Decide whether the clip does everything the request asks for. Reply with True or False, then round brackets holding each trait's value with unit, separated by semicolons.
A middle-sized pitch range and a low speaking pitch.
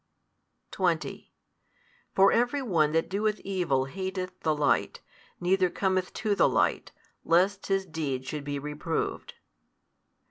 False (4.2 semitones; 185 Hz)